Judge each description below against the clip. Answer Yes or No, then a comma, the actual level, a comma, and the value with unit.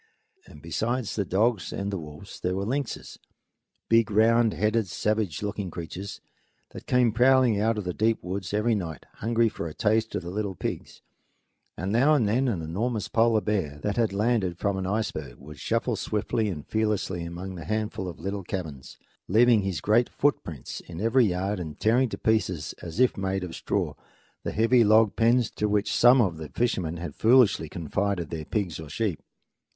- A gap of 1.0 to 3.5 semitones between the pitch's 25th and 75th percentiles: No, average, 4.1 semitones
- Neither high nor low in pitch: No, low, 105 Hz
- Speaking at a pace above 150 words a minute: Yes, average, 185 wpm